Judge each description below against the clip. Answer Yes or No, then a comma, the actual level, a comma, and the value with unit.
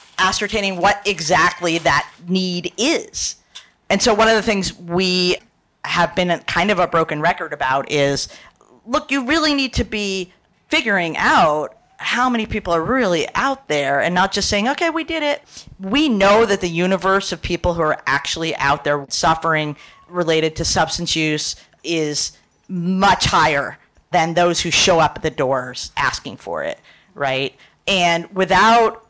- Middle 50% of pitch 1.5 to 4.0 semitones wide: No, average, 4.4 semitones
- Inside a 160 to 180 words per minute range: Yes, average, 165 wpm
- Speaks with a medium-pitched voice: Yes, medium, 180 Hz